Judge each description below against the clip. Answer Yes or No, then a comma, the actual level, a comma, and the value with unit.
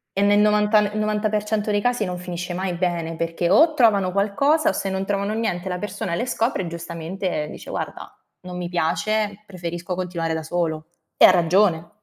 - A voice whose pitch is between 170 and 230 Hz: Yes, high, 190 Hz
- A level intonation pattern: No, average, 3.3 semitones